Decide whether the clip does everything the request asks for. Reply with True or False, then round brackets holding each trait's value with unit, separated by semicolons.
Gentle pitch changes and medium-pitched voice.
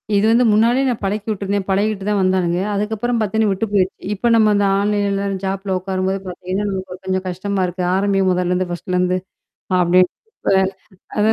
False (1.9 semitones; 195 Hz)